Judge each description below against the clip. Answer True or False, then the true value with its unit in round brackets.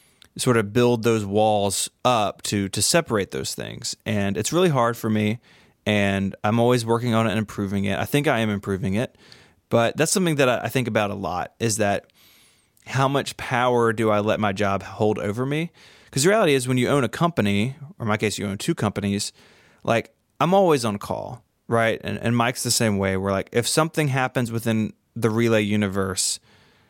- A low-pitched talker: True (115 Hz)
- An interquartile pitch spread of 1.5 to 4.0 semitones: True (3.3 semitones)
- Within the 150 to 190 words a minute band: False (205 wpm)